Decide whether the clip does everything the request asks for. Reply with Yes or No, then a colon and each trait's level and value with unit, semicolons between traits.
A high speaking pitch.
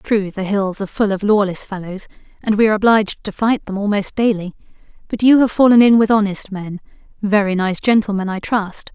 Yes: high, 205 Hz